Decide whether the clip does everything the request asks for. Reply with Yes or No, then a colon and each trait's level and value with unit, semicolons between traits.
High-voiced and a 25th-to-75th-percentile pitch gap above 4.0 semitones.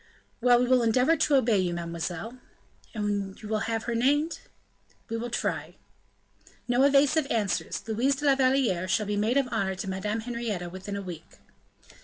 Yes: high, 225 Hz; average, 4.7 semitones